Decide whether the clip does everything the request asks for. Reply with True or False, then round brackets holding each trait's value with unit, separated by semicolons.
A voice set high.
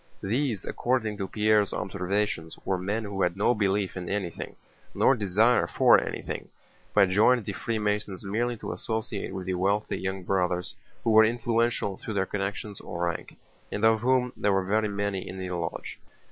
False (100 Hz)